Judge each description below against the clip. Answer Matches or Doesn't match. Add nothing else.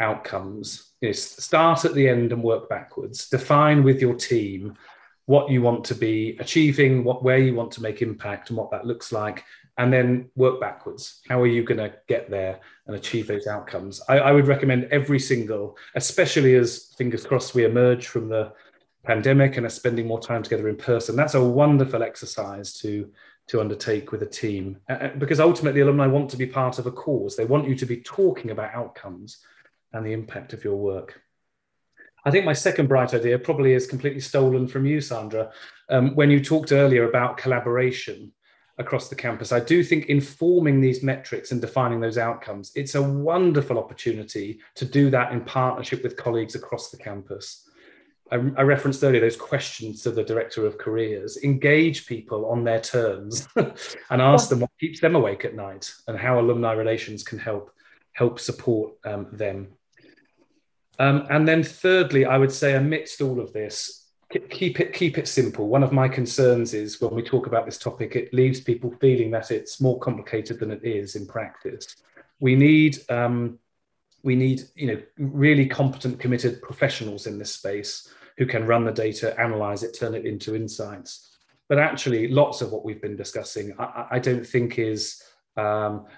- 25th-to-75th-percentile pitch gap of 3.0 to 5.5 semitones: Matches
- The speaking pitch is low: Matches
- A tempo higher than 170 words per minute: Matches